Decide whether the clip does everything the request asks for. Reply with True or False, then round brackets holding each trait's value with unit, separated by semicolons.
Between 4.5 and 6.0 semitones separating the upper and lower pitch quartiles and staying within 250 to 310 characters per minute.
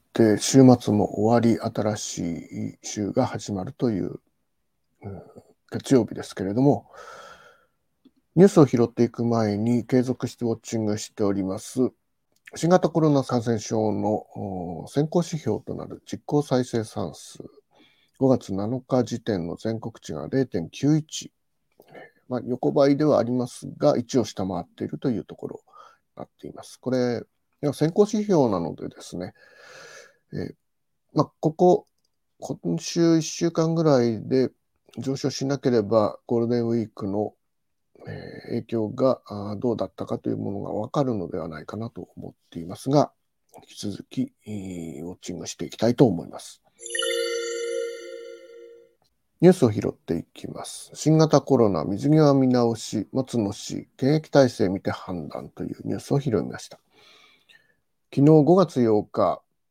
True (5.4 semitones; 270 characters per minute)